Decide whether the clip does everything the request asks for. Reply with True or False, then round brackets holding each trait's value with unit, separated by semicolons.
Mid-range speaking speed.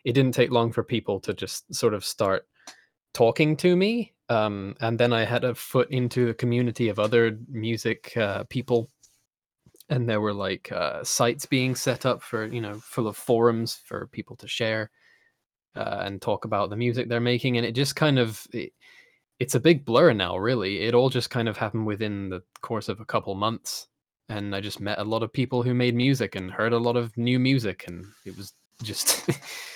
False (210 wpm)